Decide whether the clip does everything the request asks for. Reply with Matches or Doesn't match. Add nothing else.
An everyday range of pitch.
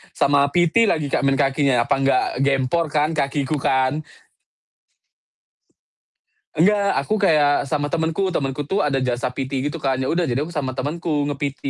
Matches